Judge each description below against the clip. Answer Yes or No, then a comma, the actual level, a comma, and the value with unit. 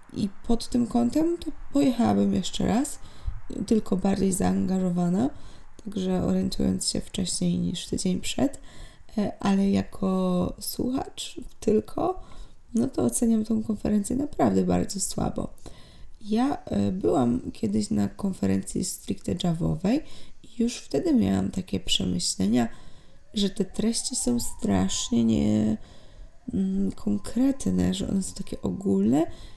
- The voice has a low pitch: No, high, 195 Hz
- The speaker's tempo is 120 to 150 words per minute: No, slow, 110 wpm